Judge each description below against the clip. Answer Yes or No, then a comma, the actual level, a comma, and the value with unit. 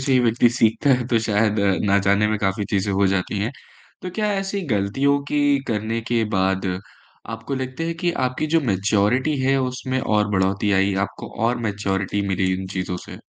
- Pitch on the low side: Yes, low, 110 Hz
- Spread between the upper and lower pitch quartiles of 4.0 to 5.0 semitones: Yes, average, 4.7 semitones